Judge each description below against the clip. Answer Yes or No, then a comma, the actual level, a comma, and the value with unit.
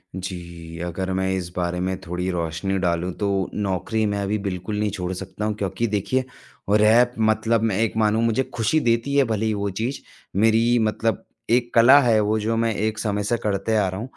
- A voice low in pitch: Yes, low, 105 Hz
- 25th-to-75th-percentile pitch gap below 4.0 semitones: Yes, average, 3.2 semitones